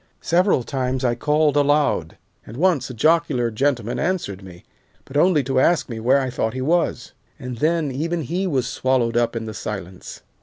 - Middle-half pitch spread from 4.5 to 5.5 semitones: Yes, average, 4.9 semitones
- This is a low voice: Yes, low, 130 Hz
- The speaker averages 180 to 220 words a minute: Yes, average, 185 wpm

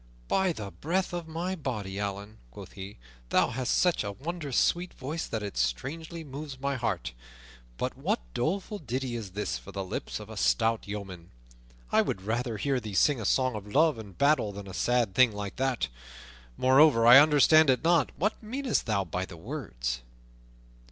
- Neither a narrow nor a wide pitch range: No, wide, 7.2 semitones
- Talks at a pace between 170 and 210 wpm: Yes, average, 185 wpm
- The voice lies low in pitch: Yes, low, 120 Hz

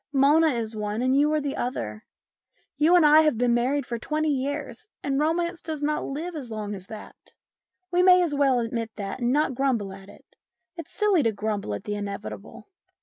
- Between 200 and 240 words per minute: Yes, fast, 205 wpm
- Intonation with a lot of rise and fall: Yes, wide, 5.8 semitones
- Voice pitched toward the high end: Yes, very high, 270 Hz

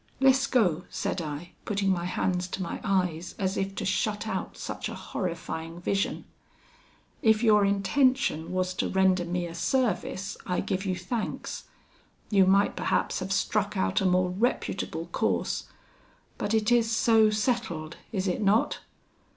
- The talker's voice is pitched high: Yes, high, 195 Hz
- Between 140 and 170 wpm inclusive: Yes, average, 150 wpm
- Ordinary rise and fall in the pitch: Yes, average, 3.0 semitones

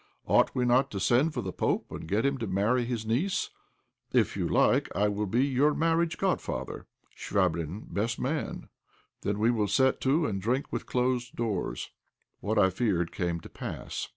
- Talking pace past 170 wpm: Yes, average, 180 wpm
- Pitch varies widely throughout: No, average, 4.5 semitones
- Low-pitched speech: Yes, low, 115 Hz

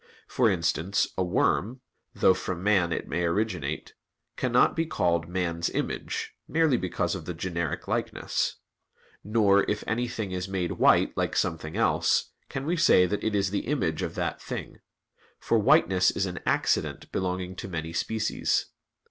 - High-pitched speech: No, very low, 95 Hz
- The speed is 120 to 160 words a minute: Yes, average, 155 wpm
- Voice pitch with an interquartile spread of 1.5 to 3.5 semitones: No, average, 4.3 semitones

